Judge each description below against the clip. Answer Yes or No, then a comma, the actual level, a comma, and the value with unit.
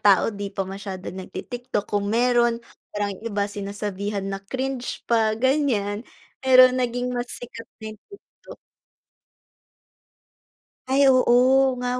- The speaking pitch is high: Yes, high, 230 Hz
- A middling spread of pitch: Yes, average, 3.7 semitones